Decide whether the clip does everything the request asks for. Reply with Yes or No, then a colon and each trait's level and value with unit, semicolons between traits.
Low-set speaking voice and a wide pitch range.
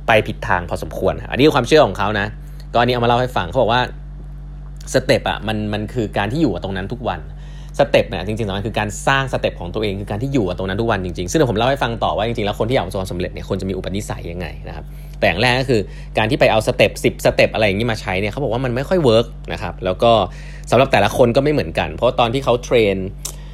Yes: low, 115 Hz; wide, 5.9 semitones